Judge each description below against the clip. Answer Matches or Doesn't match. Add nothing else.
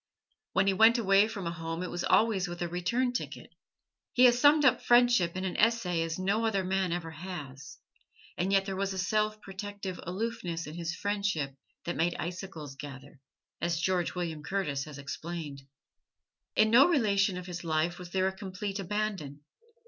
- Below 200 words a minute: Matches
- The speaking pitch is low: Doesn't match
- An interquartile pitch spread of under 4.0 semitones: Matches